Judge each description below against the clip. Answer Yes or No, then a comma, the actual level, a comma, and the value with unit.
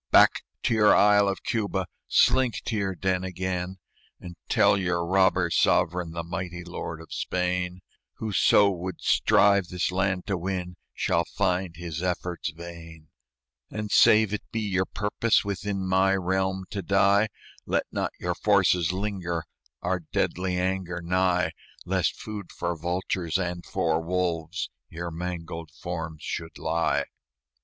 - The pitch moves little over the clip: Yes, narrow, 2.1 semitones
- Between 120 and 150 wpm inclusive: Yes, average, 140 wpm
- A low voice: Yes, very low, 90 Hz